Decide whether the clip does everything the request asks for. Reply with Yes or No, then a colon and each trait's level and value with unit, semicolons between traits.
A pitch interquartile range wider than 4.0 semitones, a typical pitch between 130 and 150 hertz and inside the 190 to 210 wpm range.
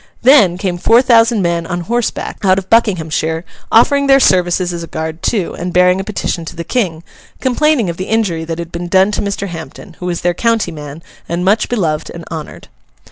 No: average, 4.7 semitones; medium, 180 Hz; fast, 205 wpm